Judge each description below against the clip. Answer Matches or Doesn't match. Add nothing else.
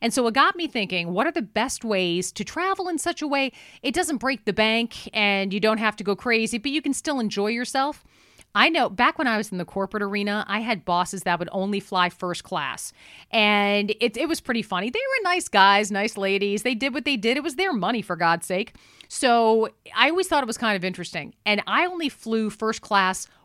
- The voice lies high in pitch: Matches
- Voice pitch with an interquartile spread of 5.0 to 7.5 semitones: Matches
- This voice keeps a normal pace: Doesn't match